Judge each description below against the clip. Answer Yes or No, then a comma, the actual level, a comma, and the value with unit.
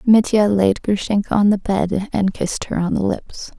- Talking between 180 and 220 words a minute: Yes, average, 200 wpm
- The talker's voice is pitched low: No, high, 200 Hz